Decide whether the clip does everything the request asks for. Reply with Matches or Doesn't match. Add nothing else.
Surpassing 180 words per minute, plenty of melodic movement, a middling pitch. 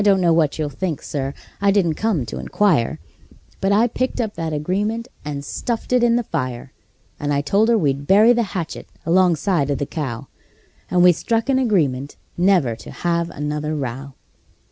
Matches